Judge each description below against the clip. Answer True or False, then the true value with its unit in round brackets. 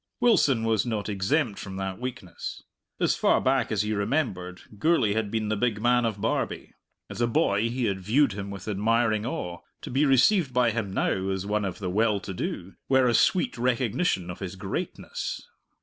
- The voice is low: True (110 Hz)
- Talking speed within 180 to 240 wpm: True (195 wpm)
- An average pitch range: True (4.0 semitones)